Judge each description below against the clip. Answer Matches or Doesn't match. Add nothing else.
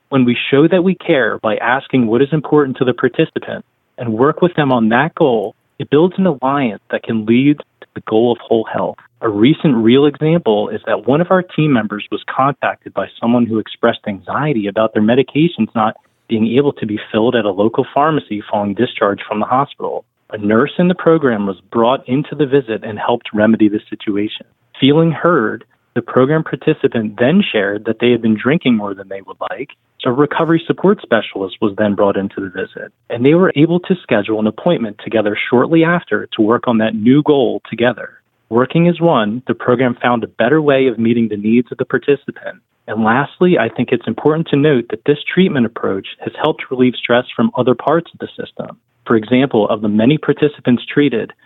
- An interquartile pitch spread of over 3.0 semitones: Matches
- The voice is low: Matches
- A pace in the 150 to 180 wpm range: Doesn't match